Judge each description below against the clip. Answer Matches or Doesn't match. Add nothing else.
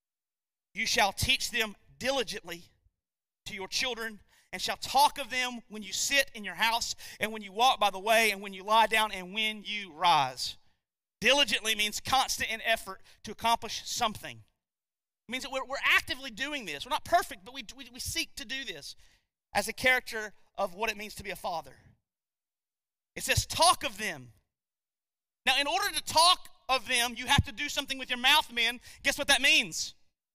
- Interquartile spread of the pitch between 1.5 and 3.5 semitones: Doesn't match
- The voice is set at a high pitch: Matches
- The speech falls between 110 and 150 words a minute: Doesn't match